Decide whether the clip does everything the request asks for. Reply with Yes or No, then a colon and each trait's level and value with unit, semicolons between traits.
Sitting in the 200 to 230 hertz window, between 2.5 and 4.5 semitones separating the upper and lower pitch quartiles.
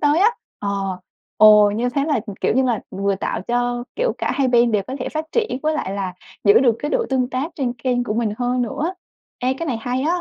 No: high, 245 Hz; average, 4.0 semitones